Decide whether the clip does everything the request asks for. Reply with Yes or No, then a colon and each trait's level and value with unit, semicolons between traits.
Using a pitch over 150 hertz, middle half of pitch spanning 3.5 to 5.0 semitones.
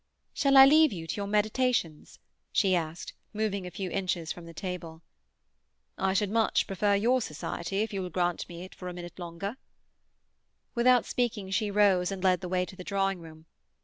No: high, 190 Hz; average, 3.1 semitones